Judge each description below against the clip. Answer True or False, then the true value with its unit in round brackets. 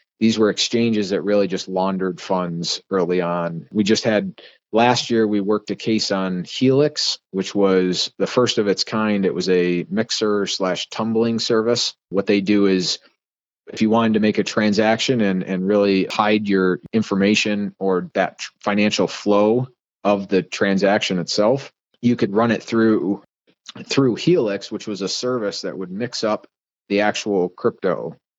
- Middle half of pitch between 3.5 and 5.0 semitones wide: False (2.7 semitones)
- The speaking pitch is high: False (105 Hz)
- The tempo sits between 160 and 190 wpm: True (165 wpm)